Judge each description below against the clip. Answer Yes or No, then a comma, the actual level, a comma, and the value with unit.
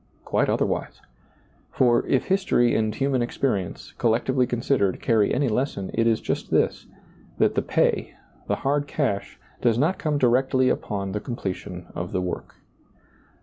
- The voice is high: No, low, 120 Hz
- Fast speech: No, average, 150 wpm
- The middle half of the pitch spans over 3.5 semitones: Yes, average, 4.4 semitones